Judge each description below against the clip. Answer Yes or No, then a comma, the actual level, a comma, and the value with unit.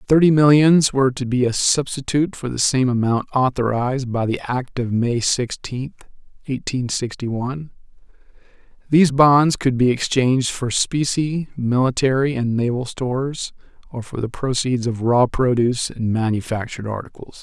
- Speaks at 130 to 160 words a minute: Yes, average, 145 wpm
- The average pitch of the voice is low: Yes, low, 130 Hz